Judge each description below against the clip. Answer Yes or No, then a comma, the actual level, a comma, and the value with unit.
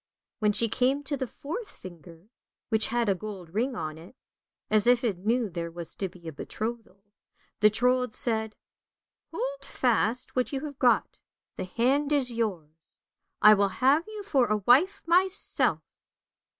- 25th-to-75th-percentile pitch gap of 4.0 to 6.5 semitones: Yes, average, 5.2 semitones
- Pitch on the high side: Yes, high, 230 Hz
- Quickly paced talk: No, average, 165 wpm